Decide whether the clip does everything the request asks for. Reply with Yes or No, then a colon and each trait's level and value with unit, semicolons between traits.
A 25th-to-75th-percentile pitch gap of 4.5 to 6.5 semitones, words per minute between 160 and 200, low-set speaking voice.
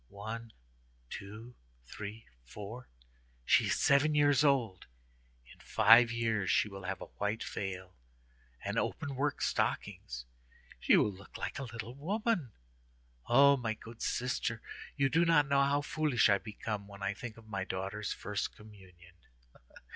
No: wide, 5.6 semitones; average, 140 wpm; low, 110 Hz